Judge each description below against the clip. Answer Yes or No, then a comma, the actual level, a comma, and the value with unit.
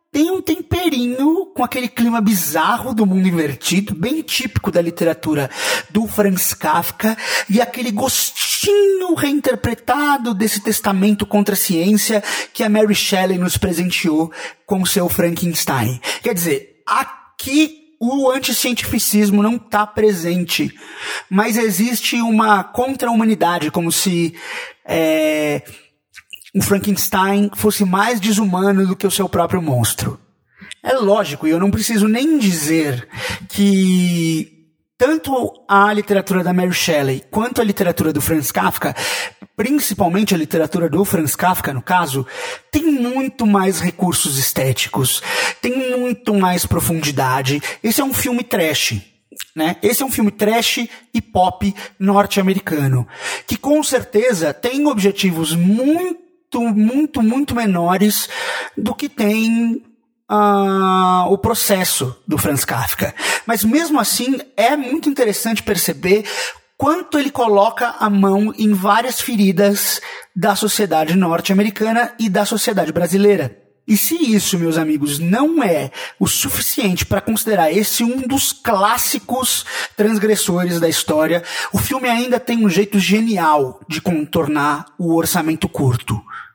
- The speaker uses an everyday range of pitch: No, wide, 5.7 semitones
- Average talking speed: Yes, average, 130 wpm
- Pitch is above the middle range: Yes, high, 205 Hz